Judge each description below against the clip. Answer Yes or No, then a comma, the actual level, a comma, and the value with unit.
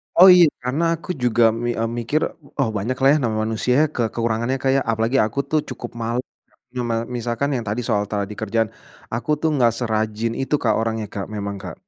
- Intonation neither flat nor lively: Yes, average, 3.2 semitones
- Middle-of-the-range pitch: No, low, 115 Hz